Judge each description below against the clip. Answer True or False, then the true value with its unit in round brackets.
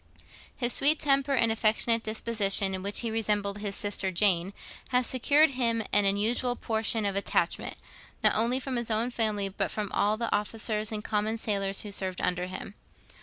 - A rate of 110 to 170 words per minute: False (180 wpm)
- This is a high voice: True (215 Hz)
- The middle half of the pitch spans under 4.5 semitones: True (2.6 semitones)